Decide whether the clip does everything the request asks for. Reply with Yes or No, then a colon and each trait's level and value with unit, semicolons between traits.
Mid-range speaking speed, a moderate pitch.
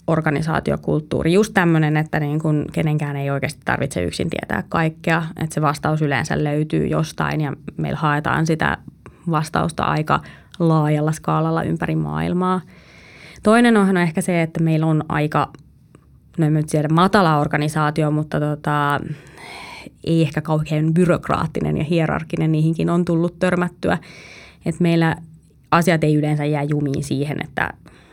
Yes: average, 140 wpm; medium, 155 Hz